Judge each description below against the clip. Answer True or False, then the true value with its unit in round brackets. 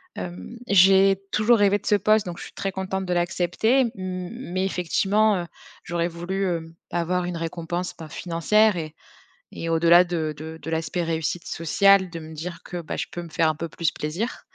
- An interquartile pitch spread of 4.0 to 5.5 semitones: False (2.8 semitones)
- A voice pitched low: False (175 Hz)